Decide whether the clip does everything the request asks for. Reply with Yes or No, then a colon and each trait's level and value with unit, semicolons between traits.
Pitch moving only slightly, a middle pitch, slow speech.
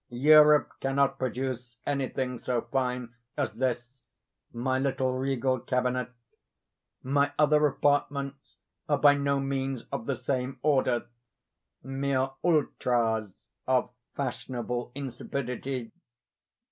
No: narrow, 2.0 semitones; low, 130 Hz; slow, 95 wpm